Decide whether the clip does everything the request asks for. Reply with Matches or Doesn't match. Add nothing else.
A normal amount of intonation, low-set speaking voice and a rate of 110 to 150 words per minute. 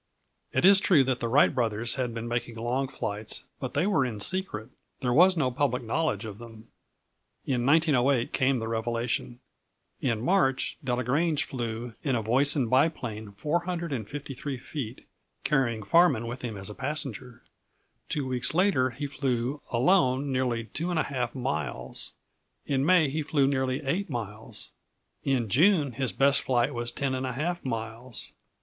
Matches